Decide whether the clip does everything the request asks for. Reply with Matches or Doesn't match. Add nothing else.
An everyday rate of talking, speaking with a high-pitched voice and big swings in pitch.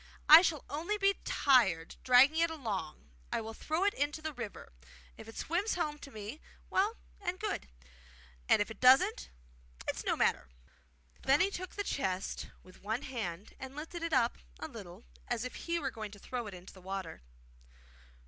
Matches